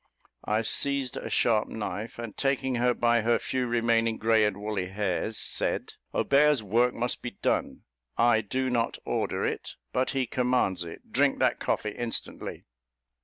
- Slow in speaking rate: No, average, 160 wpm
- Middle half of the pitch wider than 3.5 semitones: No, narrow, 2.6 semitones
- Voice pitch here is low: Yes, low, 115 Hz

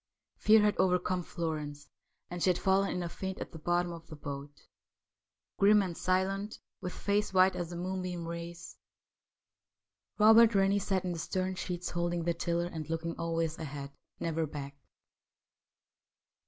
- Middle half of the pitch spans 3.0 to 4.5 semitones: No, narrow, 2.4 semitones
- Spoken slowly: No, average, 155 wpm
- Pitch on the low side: No, medium, 175 Hz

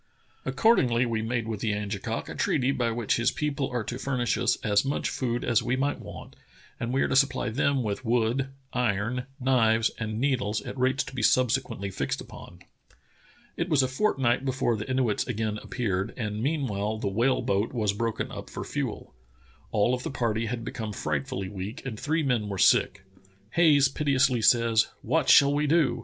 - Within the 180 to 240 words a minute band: Yes, average, 185 wpm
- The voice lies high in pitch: No, low, 120 Hz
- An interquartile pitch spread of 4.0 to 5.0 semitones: No, average, 3.6 semitones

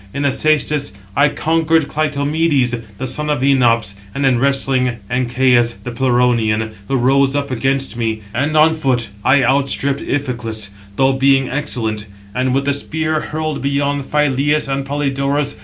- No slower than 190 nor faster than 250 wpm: No, average, 150 wpm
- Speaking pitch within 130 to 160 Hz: Yes, low, 135 Hz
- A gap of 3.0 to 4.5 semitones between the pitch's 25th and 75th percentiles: No, narrow, 2.6 semitones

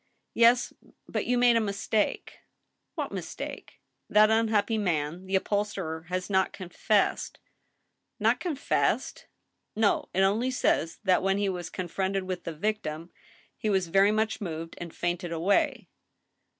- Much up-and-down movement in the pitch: No, average, 3.5 semitones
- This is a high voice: Yes, high, 195 Hz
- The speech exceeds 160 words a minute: No, average, 155 wpm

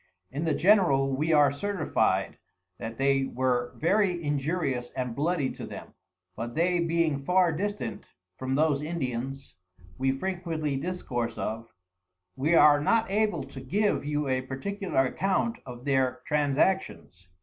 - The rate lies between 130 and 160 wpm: Yes, average, 140 wpm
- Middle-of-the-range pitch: Yes, medium, 145 Hz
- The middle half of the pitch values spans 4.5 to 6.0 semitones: Yes, average, 5.0 semitones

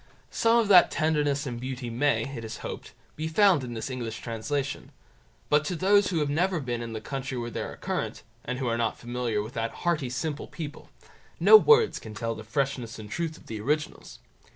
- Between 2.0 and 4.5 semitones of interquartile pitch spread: No, average, 5.2 semitones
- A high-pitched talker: No, low, 135 Hz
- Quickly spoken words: Yes, fast, 210 wpm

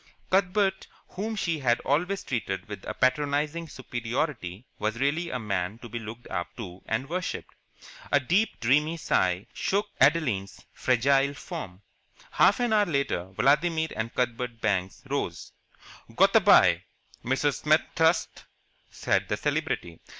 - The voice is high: No, low, 135 Hz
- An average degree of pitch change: No, wide, 6.9 semitones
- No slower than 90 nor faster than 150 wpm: Yes, average, 140 wpm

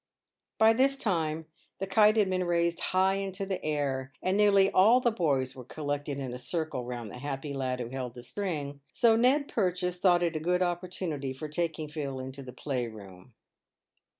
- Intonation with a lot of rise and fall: Yes, wide, 6.1 semitones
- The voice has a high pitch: No, medium, 160 Hz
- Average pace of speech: Yes, average, 185 wpm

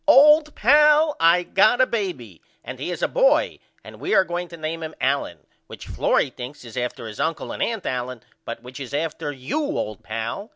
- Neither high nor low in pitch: Yes, medium, 165 Hz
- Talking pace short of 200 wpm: No, fast, 205 wpm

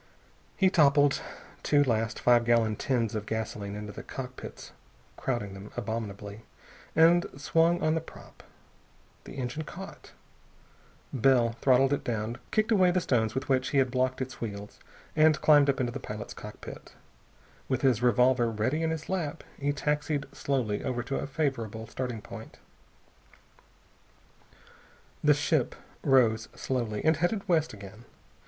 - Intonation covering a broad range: No, average, 4.8 semitones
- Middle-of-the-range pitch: No, low, 130 Hz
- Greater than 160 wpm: No, average, 145 wpm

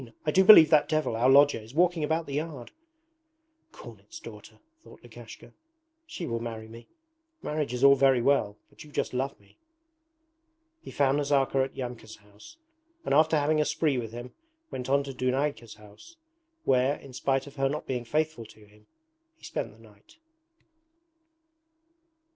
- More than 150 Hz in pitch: No, low, 135 Hz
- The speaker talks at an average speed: Yes, average, 165 wpm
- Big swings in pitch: No, average, 4.3 semitones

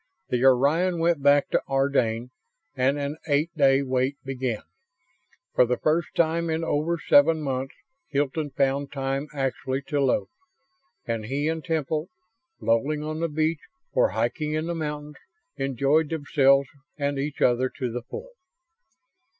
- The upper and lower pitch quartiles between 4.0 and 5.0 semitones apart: No, average, 2.7 semitones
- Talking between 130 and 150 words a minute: Yes, average, 145 wpm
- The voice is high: No, medium, 145 Hz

